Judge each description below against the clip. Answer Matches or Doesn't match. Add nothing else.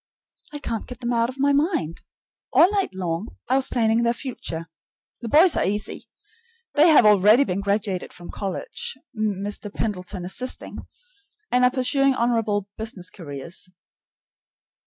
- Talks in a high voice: Matches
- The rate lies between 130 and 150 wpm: Matches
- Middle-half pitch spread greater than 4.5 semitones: Matches